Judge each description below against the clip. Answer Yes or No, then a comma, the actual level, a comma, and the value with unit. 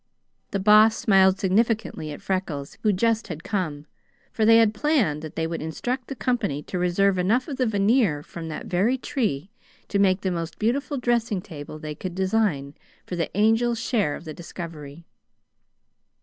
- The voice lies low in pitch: No, high, 195 Hz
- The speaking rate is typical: Yes, average, 175 wpm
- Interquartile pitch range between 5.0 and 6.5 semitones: Yes, wide, 5.5 semitones